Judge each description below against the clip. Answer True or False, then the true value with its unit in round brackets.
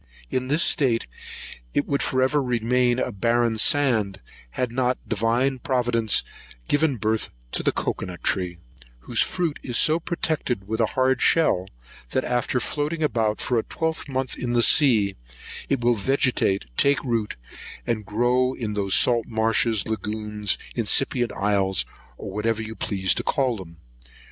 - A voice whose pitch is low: True (120 Hz)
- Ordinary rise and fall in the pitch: True (3.6 semitones)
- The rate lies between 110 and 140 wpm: False (155 wpm)